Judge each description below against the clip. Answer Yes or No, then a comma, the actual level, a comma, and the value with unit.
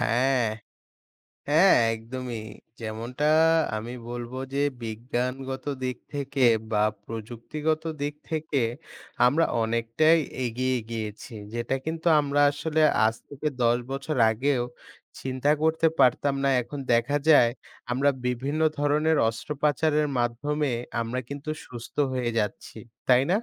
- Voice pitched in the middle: No, low, 130 Hz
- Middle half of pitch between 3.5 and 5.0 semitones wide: Yes, average, 3.8 semitones